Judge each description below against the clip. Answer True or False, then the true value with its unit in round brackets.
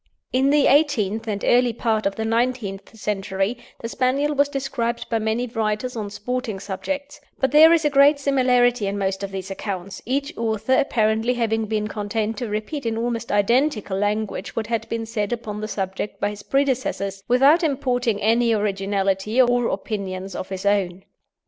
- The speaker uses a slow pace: False (175 wpm)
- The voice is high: True (225 Hz)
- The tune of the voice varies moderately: True (3.7 semitones)